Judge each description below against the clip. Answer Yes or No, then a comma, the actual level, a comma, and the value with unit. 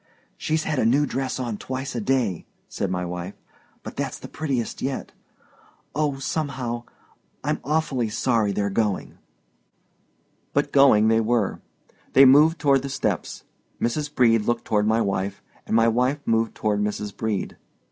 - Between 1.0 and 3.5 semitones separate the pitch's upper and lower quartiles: No, average, 4.2 semitones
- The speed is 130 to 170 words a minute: Yes, average, 150 wpm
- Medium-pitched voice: No, low, 120 Hz